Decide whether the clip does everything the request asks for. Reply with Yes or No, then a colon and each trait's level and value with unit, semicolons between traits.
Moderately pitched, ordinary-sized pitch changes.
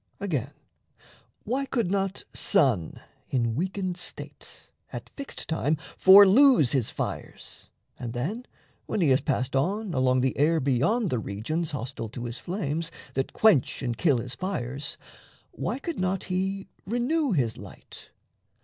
No: medium, 160 Hz; wide, 7.5 semitones